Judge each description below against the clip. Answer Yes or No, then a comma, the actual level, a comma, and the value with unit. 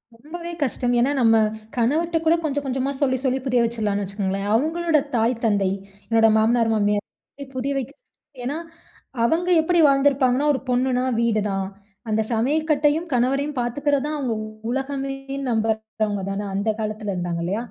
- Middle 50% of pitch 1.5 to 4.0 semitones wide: No, average, 4.4 semitones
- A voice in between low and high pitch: No, very high, 250 Hz